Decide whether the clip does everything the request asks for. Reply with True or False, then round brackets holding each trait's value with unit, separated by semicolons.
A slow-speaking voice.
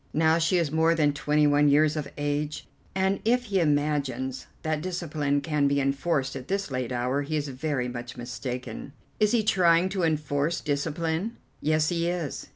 False (175 wpm)